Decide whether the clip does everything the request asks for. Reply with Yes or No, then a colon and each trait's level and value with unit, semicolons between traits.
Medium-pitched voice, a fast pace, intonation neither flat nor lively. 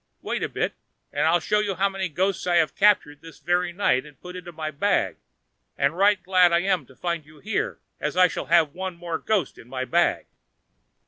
Yes: medium, 175 Hz; fast, 215 wpm; average, 3.5 semitones